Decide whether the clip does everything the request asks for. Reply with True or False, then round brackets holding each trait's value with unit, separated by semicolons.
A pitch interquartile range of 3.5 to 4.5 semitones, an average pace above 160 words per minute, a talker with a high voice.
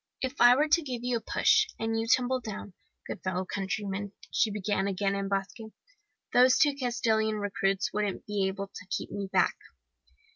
True (3.8 semitones; 180 wpm; 210 Hz)